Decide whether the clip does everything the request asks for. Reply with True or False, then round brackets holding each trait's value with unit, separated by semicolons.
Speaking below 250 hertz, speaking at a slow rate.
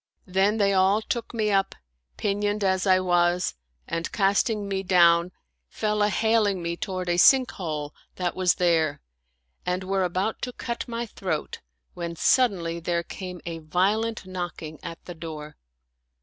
False (185 Hz; 155 wpm)